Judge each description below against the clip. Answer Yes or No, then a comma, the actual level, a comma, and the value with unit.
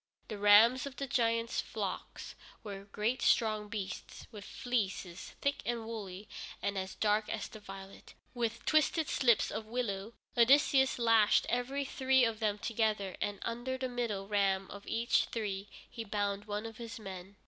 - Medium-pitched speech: No, high, 220 Hz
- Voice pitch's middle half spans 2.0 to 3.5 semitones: Yes, average, 3.0 semitones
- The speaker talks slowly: No, average, 160 wpm